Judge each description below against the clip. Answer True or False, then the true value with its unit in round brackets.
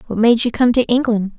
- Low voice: False (230 Hz)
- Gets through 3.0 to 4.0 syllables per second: False (6.0 syllables/s)